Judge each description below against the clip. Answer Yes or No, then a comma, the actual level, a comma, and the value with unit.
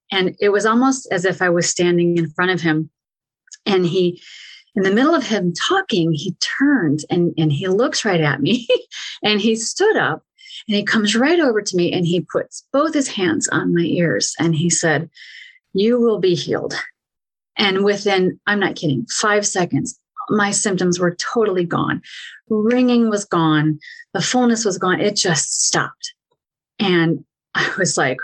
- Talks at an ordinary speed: Yes, average, 175 wpm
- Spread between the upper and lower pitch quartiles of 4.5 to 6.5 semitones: Yes, average, 4.8 semitones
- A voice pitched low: No, high, 195 Hz